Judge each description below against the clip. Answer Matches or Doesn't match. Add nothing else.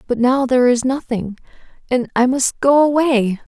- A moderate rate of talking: Matches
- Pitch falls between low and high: Doesn't match